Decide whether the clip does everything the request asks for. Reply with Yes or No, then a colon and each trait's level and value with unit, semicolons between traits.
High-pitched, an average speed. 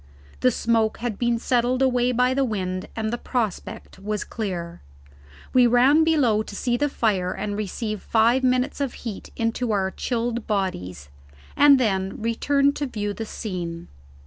Yes: high, 230 Hz; average, 165 wpm